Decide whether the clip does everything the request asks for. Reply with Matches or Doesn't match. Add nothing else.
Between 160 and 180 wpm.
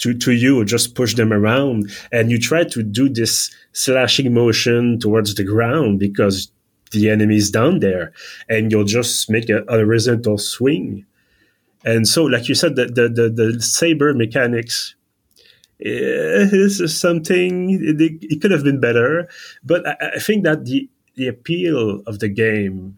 Matches